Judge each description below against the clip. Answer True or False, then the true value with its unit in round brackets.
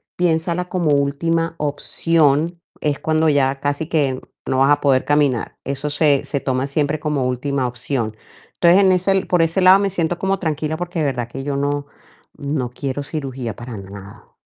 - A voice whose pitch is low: False (145 Hz)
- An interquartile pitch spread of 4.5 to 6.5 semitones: False (3.5 semitones)